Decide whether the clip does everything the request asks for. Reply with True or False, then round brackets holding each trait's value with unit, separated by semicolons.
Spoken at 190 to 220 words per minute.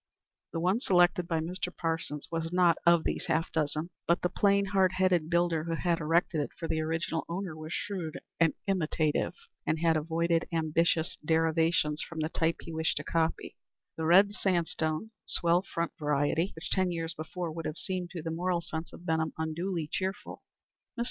False (180 wpm)